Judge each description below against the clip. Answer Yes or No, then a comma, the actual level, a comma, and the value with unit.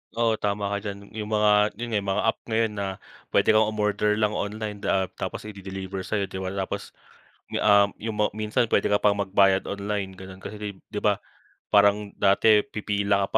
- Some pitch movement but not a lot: No, narrow, 1.2 semitones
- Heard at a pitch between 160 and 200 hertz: No, low, 105 Hz